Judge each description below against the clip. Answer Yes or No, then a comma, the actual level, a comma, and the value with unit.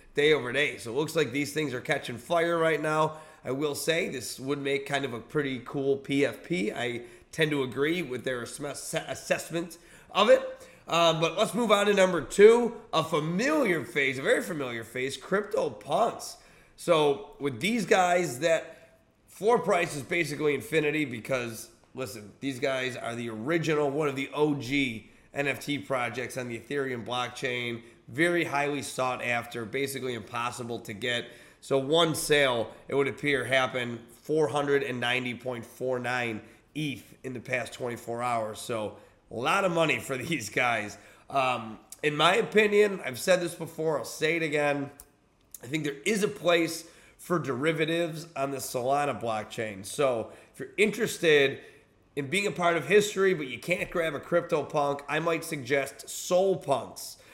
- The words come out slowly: No, average, 160 wpm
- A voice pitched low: No, medium, 145 Hz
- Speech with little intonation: No, average, 5.0 semitones